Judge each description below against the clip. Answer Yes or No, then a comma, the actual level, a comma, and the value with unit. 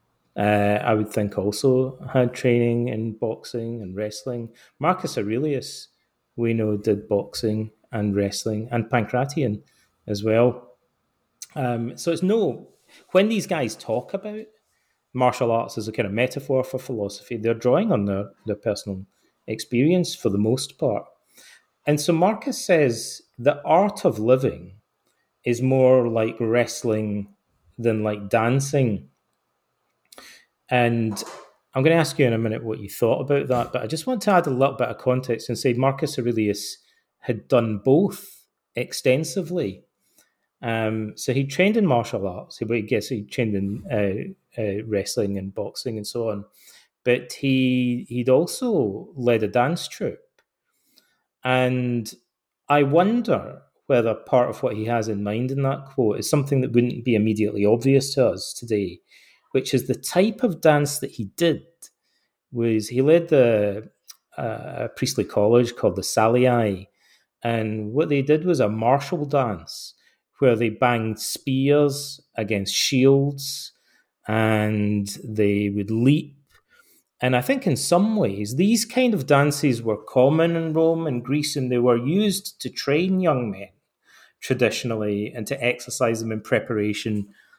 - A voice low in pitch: Yes, low, 125 Hz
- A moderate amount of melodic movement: Yes, average, 4.6 semitones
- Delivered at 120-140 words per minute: No, average, 150 wpm